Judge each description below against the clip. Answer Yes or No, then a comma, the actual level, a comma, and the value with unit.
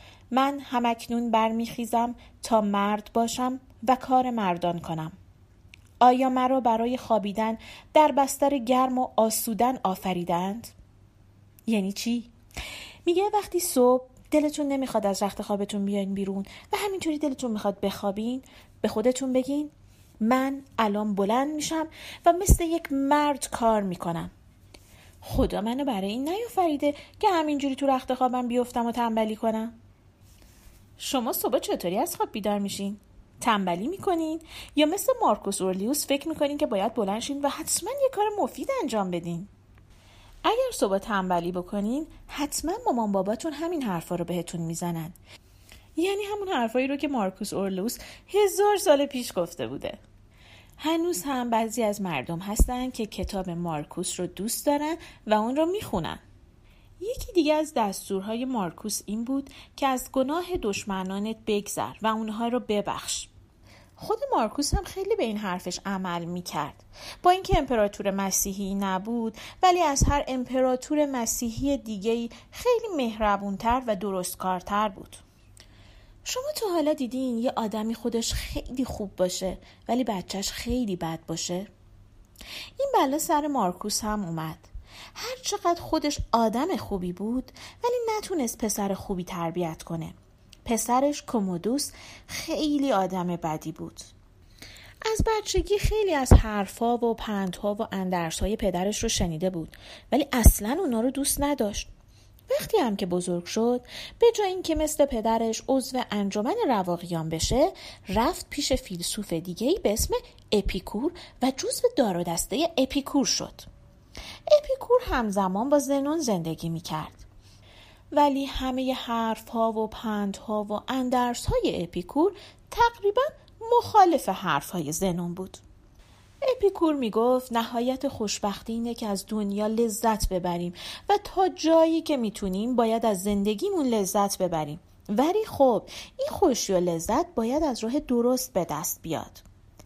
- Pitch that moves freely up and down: Yes, wide, 7.1 semitones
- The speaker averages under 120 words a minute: No, average, 135 wpm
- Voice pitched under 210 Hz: No, high, 230 Hz